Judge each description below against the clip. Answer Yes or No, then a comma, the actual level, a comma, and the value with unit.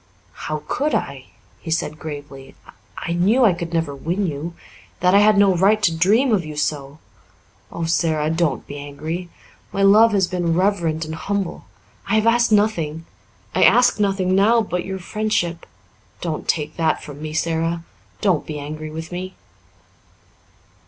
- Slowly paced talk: No, average, 165 wpm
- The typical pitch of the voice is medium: Yes, medium, 170 Hz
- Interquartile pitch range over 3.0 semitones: Yes, average, 4.2 semitones